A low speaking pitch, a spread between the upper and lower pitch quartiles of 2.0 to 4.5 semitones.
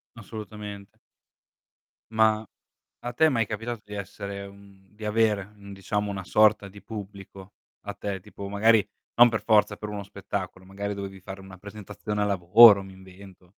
No: low, 100 Hz; narrow, 1.6 semitones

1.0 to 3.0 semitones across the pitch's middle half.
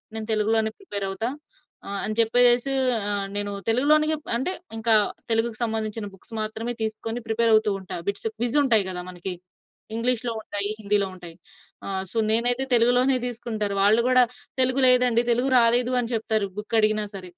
Yes: average, 2.7 semitones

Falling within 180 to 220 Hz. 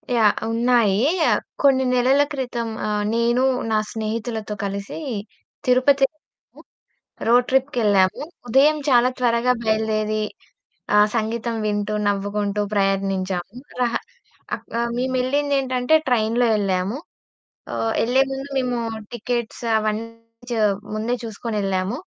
No: high, 230 Hz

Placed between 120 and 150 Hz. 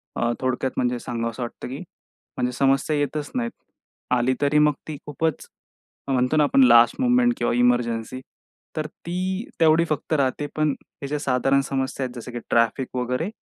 Yes: low, 135 Hz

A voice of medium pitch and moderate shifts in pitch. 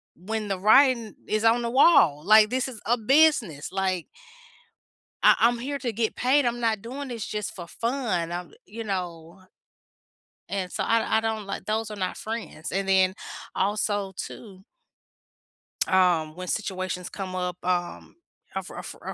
No: high, 210 Hz; average, 4.0 semitones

